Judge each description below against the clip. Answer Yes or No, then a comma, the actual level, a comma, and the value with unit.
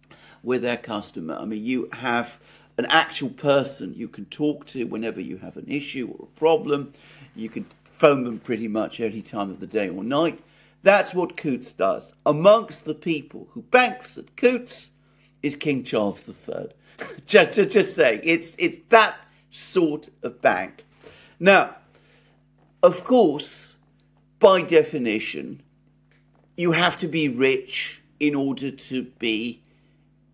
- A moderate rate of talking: Yes, average, 145 wpm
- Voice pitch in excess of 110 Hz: Yes, medium, 140 Hz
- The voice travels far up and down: Yes, wide, 6.5 semitones